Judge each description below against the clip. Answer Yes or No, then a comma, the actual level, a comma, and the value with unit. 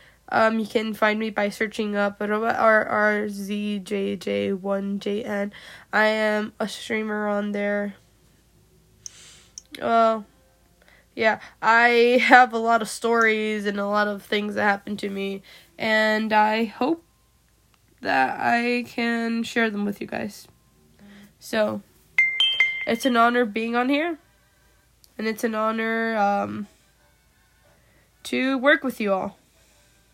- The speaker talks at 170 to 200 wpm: No, slow, 135 wpm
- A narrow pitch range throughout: Yes, narrow, 2.1 semitones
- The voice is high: Yes, high, 215 Hz